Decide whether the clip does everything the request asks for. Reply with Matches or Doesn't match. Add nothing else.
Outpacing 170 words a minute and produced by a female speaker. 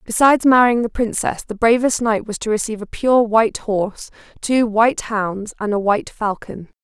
Matches